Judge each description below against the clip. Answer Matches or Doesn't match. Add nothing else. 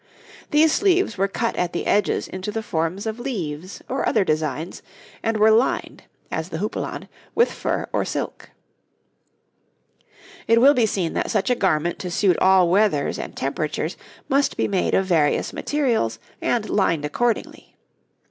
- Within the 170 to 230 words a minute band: Doesn't match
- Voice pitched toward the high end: Matches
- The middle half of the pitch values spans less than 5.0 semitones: Doesn't match